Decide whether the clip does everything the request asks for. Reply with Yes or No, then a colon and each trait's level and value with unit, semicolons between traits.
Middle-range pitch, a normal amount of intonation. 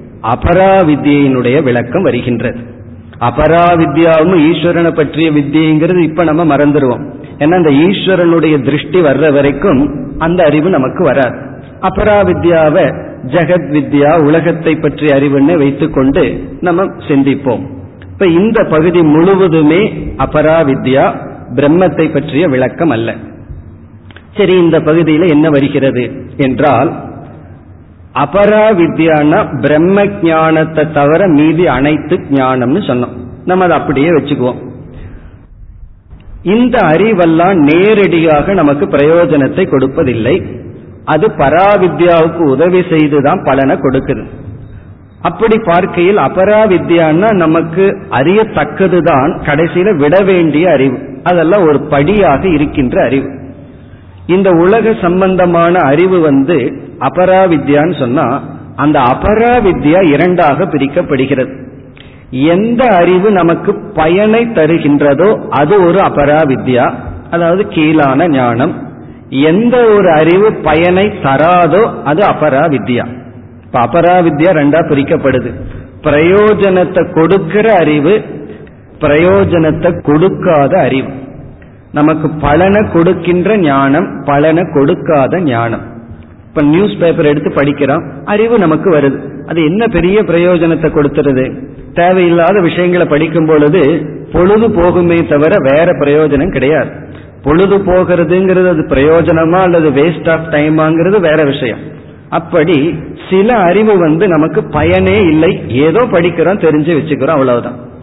Yes: medium, 155 Hz; average, 4.3 semitones